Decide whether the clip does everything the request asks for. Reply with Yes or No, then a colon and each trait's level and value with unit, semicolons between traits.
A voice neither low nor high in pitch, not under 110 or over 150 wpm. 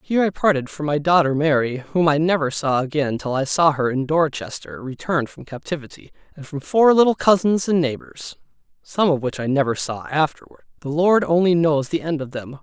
No: medium, 150 Hz; fast, 205 wpm